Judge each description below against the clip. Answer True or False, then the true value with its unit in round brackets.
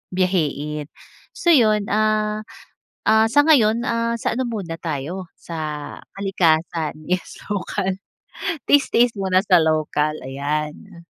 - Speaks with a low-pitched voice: False (190 Hz)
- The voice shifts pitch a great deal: True (5.7 semitones)